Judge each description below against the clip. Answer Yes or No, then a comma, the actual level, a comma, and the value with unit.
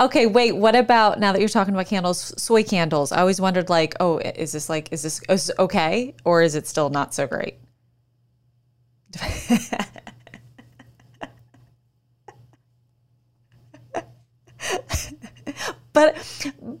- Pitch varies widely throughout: Yes, wide, 8.5 semitones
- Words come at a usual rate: No, slow, 120 wpm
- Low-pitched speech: No, medium, 155 Hz